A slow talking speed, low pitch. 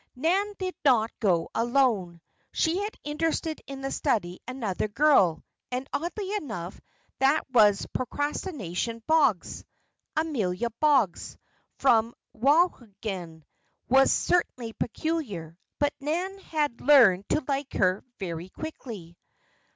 No: slow, 110 wpm; very high, 255 Hz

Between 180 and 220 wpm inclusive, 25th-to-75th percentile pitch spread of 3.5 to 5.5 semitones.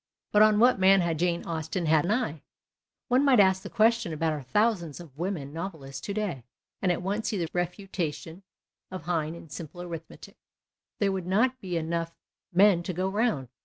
Yes: average, 185 wpm; average, 3.8 semitones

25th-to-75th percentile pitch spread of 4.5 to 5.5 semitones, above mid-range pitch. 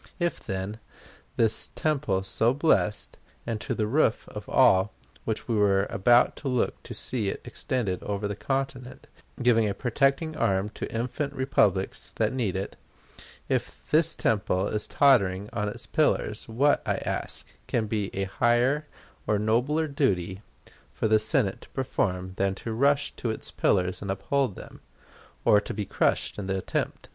No: average, 5.1 semitones; low, 110 Hz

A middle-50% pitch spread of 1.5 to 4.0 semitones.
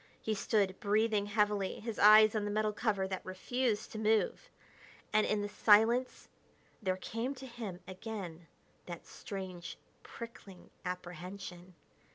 Yes: average, 2.8 semitones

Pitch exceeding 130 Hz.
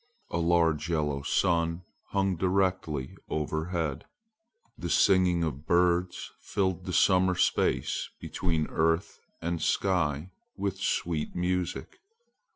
No: very low, 85 Hz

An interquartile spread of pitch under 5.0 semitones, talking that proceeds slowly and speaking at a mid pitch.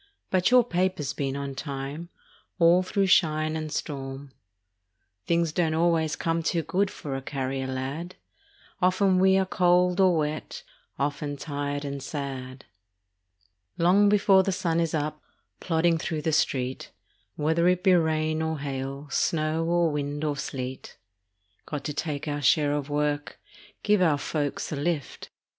No: average, 3.4 semitones; average, 150 wpm; medium, 155 Hz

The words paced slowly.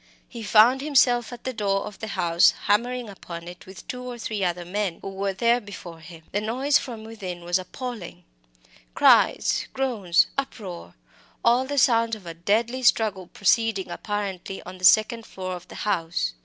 No: average, 175 wpm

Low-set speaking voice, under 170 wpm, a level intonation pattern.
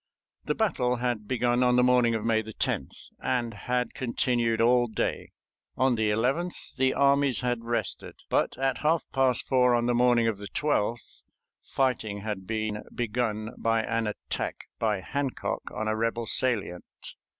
Yes: low, 120 Hz; average, 160 wpm; narrow, 2.3 semitones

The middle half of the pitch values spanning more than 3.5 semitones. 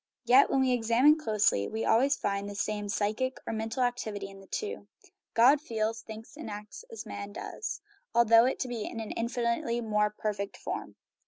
No: average, 2.9 semitones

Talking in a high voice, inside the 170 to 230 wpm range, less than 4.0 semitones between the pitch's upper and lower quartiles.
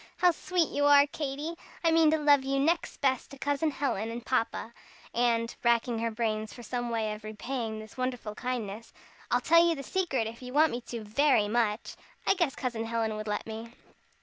No: high, 245 Hz; fast, 205 wpm; average, 4.3 semitones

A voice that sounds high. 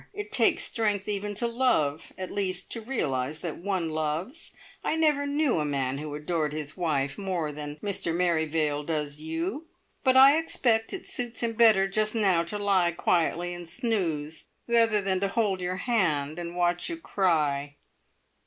No: medium, 180 Hz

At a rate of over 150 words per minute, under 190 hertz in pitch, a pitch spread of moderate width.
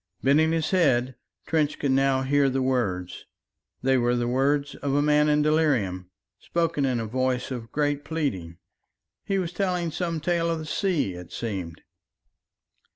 Yes: average, 160 wpm; medium, 140 Hz; average, 4.4 semitones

